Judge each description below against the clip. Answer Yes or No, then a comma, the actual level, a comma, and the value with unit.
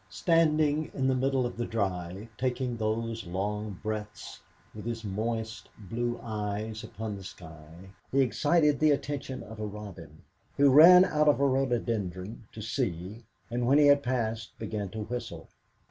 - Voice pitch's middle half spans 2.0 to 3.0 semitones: No, average, 4.2 semitones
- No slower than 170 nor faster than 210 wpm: No, average, 160 wpm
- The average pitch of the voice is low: Yes, low, 115 Hz